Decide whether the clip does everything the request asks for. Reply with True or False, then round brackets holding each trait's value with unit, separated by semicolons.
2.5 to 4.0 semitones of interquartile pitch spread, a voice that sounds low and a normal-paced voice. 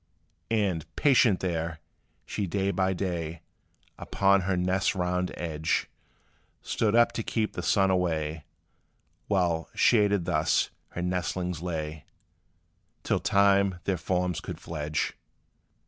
False (2.8 semitones; 90 Hz; 115 wpm)